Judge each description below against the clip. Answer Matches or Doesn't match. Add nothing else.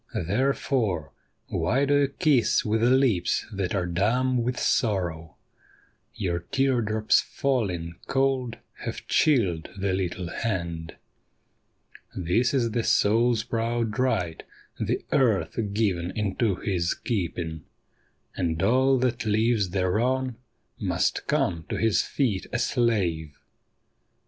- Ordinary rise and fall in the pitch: Doesn't match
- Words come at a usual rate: Doesn't match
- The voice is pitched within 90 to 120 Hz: Matches